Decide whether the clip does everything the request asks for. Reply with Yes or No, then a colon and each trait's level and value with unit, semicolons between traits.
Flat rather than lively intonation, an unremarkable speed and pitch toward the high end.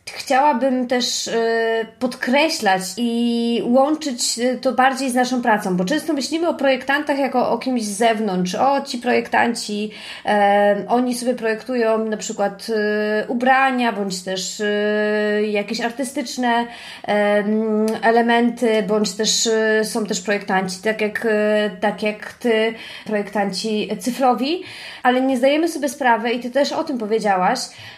No: average, 3.1 semitones; average, 120 wpm; high, 230 Hz